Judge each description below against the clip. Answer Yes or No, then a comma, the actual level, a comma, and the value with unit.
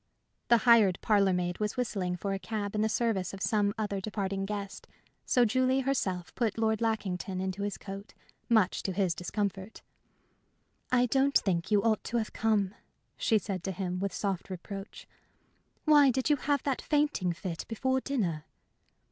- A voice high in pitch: Yes, high, 205 Hz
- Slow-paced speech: No, average, 170 wpm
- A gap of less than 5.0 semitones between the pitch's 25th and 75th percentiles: Yes, average, 3.5 semitones